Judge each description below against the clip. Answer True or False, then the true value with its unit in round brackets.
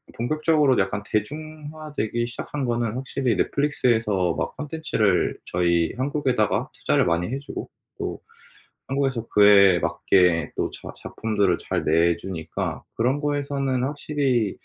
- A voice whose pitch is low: True (120 Hz)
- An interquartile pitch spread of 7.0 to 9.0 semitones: False (6.3 semitones)